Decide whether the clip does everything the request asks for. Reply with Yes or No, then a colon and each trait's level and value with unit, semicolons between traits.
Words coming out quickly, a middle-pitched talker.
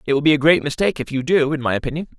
Yes: fast, 330 wpm; medium, 145 Hz